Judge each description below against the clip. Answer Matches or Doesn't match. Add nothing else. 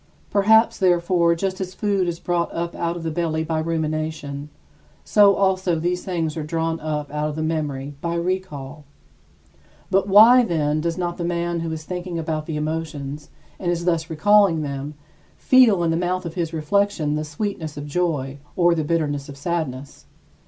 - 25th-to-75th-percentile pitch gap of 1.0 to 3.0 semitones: Matches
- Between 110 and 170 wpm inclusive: Doesn't match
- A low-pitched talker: Doesn't match